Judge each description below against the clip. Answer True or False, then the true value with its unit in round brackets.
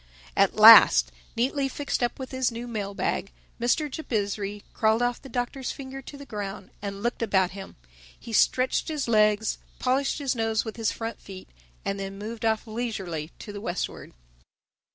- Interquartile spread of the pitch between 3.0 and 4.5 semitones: True (4.0 semitones)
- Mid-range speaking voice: False (225 Hz)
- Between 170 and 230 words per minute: True (175 wpm)